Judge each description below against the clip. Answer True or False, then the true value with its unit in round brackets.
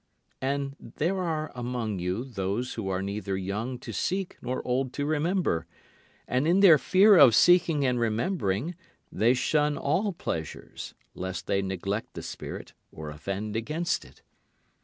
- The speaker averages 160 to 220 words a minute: False (150 wpm)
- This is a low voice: True (125 Hz)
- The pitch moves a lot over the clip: True (7.9 semitones)